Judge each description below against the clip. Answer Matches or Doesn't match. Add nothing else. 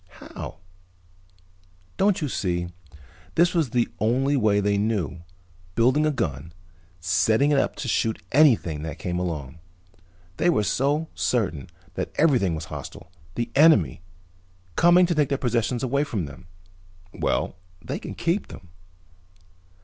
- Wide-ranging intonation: Matches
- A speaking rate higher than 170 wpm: Doesn't match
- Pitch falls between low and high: Doesn't match